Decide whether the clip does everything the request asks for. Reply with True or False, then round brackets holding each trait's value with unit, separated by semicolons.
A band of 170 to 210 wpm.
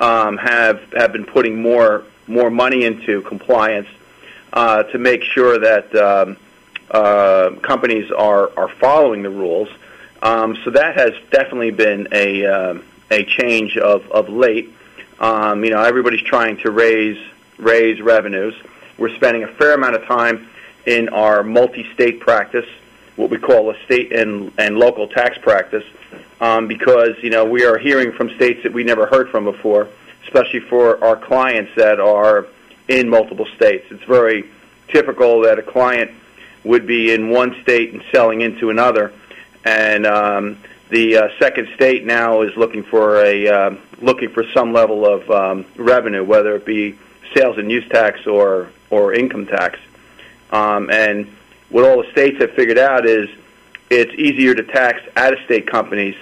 False (160 wpm)